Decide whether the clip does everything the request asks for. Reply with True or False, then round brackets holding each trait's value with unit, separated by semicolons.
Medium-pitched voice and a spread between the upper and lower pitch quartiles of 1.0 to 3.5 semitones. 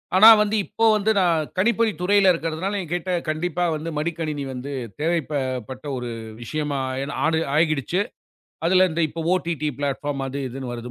False (160 Hz; 4.2 semitones)